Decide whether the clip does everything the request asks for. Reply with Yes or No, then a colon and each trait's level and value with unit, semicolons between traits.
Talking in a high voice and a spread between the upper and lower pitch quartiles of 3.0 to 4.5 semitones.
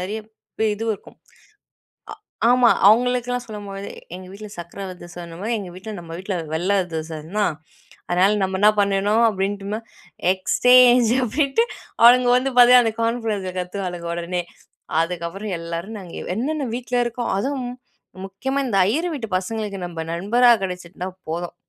No: high, 205 Hz; average, 4.9 semitones